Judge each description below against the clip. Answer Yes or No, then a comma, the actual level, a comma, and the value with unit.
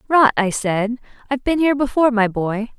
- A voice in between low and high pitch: No, high, 240 Hz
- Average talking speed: Yes, average, 195 wpm